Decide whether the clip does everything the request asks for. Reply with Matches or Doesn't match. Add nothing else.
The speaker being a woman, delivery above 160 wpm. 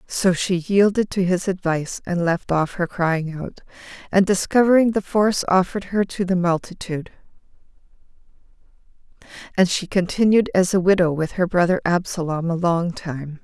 Doesn't match